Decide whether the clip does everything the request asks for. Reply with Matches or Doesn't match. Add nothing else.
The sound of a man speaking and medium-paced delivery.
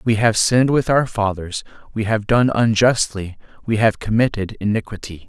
Matches